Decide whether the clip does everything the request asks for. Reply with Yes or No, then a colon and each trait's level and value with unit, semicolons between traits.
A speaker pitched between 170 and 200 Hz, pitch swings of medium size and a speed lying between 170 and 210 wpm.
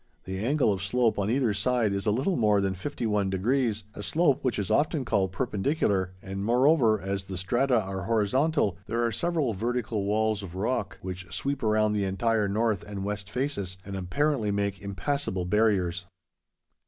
No: low, 105 Hz; average, 4.3 semitones; average, 180 wpm